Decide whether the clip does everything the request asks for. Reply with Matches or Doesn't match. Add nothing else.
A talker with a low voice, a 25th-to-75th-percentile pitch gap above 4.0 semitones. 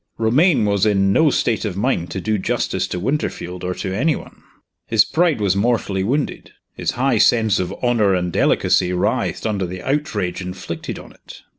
Matches